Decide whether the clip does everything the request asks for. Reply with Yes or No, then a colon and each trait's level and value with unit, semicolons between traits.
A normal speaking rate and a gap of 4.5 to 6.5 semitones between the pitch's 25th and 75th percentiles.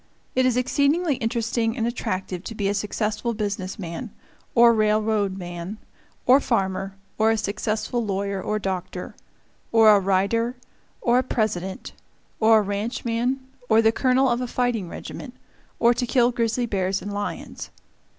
No: average, 150 wpm; average, 3.2 semitones